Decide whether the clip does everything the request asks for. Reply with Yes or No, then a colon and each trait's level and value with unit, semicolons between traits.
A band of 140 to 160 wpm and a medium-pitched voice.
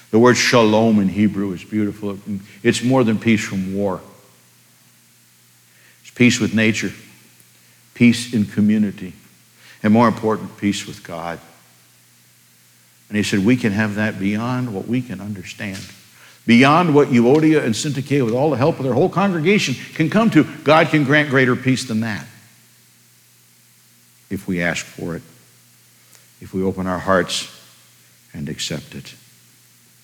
No: average, 150 wpm; low, 105 Hz